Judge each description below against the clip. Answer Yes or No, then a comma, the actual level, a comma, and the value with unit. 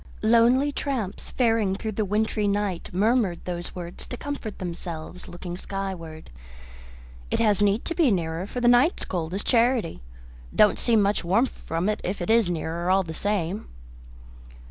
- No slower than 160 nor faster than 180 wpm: Yes, average, 165 wpm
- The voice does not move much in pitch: No, average, 4.5 semitones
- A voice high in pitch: Yes, high, 200 Hz